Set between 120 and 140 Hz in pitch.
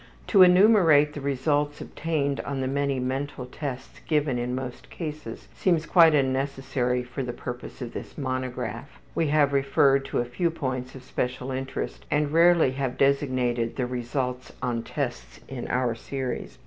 Yes: low, 135 Hz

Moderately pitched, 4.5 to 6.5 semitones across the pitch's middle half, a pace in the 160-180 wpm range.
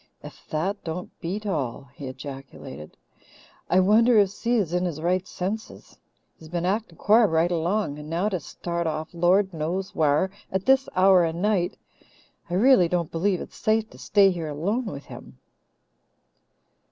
No: medium, 180 Hz; average, 3.9 semitones; average, 165 wpm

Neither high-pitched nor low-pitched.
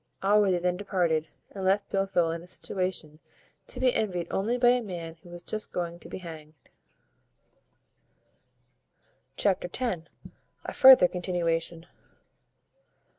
Yes: medium, 180 Hz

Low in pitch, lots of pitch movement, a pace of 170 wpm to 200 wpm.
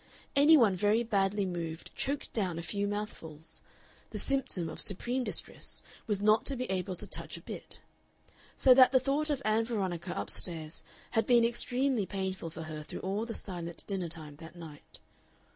No: high, 200 Hz; wide, 5.8 semitones; average, 180 wpm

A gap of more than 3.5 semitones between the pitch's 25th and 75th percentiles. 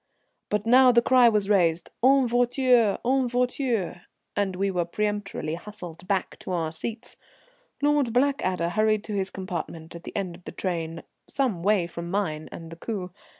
Yes: wide, 5.6 semitones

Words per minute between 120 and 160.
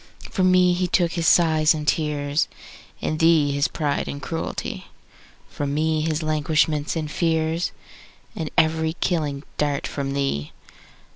Yes: average, 145 wpm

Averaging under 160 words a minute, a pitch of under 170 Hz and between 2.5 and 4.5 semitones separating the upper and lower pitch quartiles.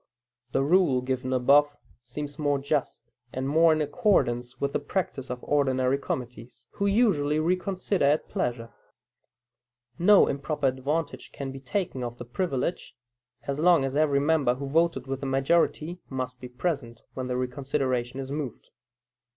Yes: average, 150 wpm; medium, 140 Hz; average, 3.4 semitones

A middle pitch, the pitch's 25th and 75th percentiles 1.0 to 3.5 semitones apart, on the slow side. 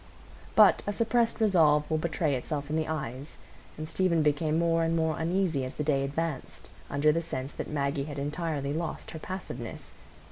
No: medium, 155 Hz; average, 2.7 semitones; average, 180 wpm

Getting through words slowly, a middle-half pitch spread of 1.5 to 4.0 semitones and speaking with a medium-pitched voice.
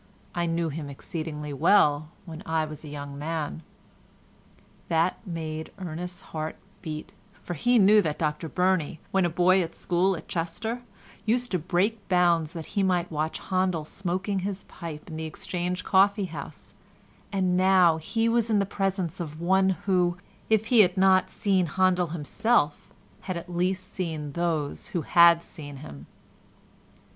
No: average, 155 wpm; average, 3.1 semitones; medium, 175 Hz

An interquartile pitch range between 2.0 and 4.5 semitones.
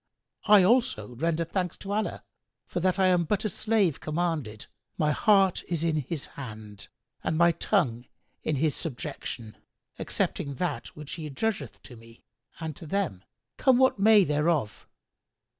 No: wide, 5.6 semitones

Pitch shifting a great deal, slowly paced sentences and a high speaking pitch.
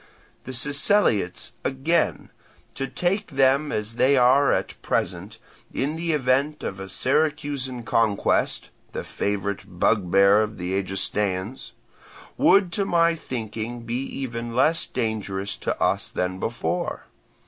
No: wide, 6.1 semitones; slow, 125 wpm; low, 125 Hz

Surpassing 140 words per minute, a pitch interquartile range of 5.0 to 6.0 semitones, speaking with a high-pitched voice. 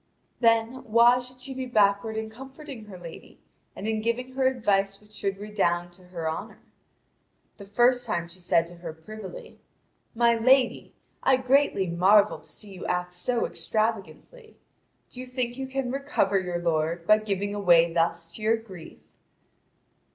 Yes: average, 165 wpm; wide, 5.6 semitones; high, 215 Hz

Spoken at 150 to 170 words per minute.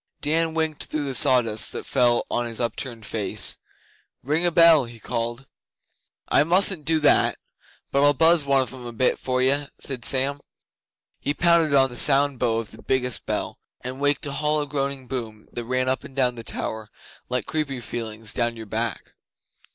No: average, 185 wpm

